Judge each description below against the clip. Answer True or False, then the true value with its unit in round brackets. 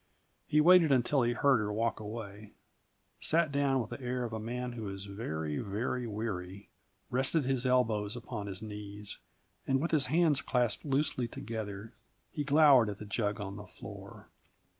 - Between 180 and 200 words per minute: False (170 wpm)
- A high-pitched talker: False (115 Hz)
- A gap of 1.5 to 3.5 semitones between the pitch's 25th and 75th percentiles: False (4.4 semitones)